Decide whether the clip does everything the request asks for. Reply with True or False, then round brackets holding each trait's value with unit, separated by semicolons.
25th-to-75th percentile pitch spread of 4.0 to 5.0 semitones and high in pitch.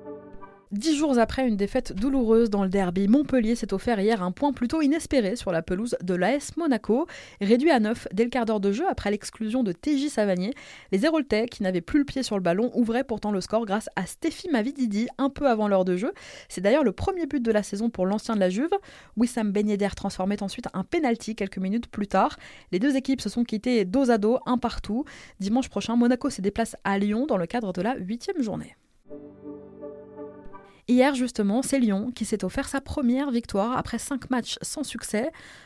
True (4.5 semitones; 230 Hz)